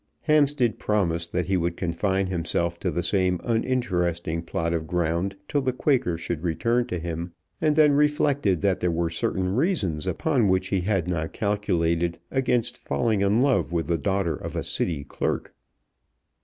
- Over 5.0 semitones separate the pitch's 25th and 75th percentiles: Yes, wide, 5.6 semitones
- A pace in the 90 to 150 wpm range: No, average, 170 wpm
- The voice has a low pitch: Yes, very low, 95 Hz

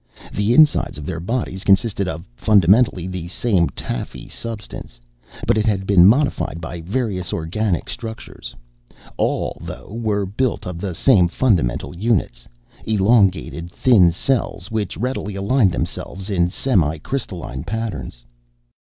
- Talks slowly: Yes, slow, 130 wpm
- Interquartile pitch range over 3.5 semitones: Yes, average, 4.4 semitones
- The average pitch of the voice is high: No, low, 100 Hz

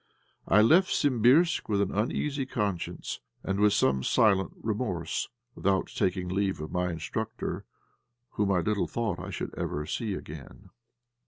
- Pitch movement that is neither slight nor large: Yes, average, 3.7 semitones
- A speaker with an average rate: Yes, average, 145 wpm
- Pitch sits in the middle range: No, low, 100 Hz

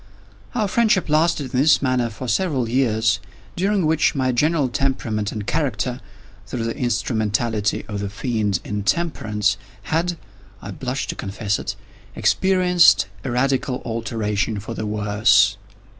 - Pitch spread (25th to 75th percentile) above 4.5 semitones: Yes, wide, 5.4 semitones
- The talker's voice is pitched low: Yes, low, 120 Hz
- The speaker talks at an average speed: No, slow, 130 wpm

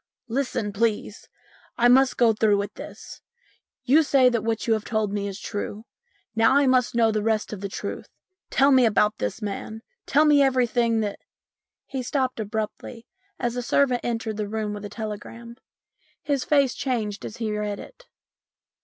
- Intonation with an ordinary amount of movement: Yes, average, 3.2 semitones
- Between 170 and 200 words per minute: Yes, average, 180 wpm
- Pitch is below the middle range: No, high, 225 Hz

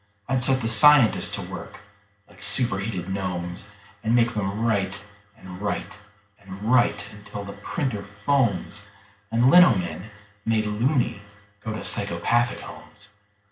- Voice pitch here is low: Yes, low, 105 Hz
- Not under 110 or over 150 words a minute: Yes, slow, 135 wpm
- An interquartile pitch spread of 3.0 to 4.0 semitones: Yes, average, 3.3 semitones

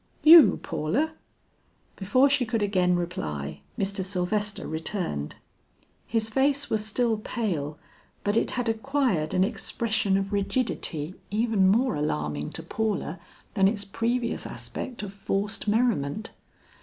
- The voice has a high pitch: Yes, high, 205 Hz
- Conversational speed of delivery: No, slow, 125 wpm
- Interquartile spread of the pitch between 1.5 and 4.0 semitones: No, average, 4.4 semitones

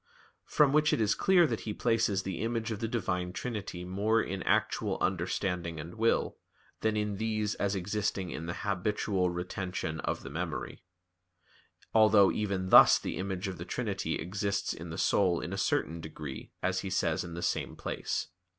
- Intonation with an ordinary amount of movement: Yes, average, 3.3 semitones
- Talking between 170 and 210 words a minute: Yes, average, 180 wpm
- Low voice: Yes, very low, 95 Hz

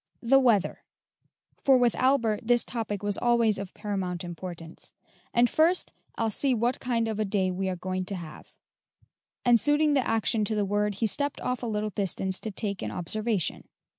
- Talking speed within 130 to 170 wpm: No, average, 185 wpm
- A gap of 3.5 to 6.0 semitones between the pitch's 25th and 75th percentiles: Yes, average, 3.8 semitones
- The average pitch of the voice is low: No, high, 215 Hz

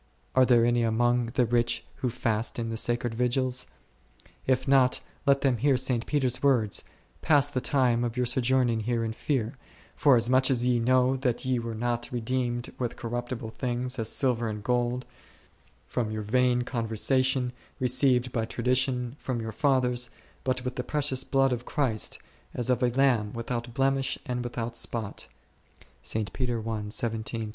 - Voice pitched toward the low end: Yes, low, 125 Hz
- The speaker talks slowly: No, average, 155 wpm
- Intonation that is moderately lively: No, narrow, 1.7 semitones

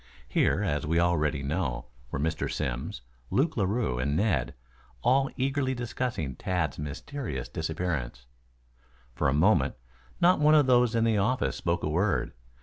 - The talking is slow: No, average, 145 wpm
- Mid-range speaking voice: No, very low, 85 Hz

